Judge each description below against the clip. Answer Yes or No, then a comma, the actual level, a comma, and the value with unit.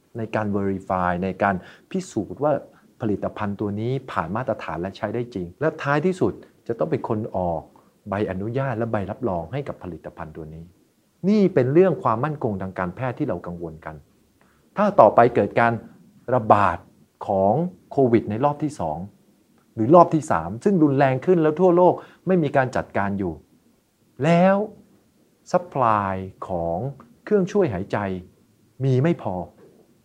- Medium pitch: No, low, 115 Hz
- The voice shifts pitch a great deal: Yes, wide, 8.1 semitones